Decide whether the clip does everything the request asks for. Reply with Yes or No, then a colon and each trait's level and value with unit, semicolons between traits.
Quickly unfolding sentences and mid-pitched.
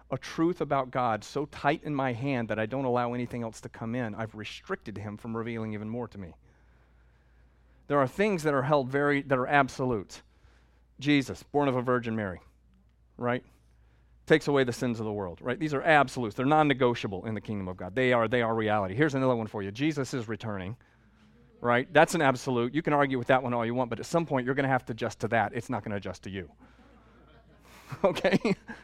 No: fast, 220 wpm; low, 120 Hz